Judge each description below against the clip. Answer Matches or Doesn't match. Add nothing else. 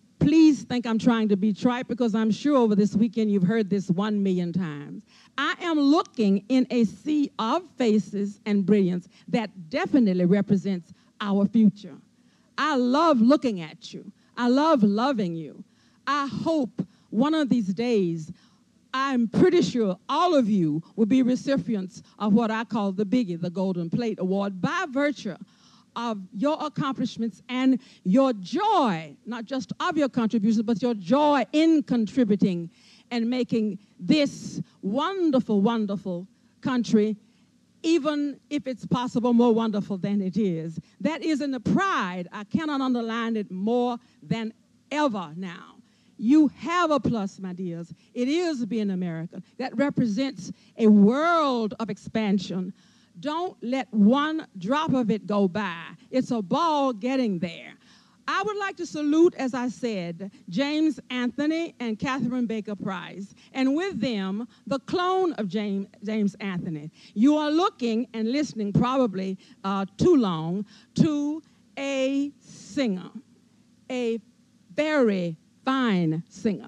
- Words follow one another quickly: Doesn't match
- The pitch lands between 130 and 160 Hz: Doesn't match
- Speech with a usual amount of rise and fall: Matches